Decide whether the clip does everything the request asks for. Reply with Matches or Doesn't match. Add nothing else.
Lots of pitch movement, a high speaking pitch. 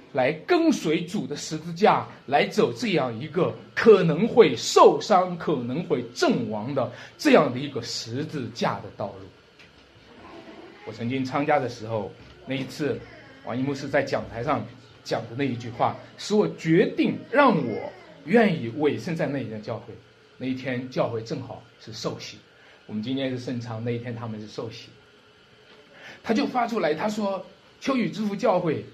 Doesn't match